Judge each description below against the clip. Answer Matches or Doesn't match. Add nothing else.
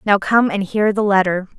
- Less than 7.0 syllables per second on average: Matches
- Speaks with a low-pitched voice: Doesn't match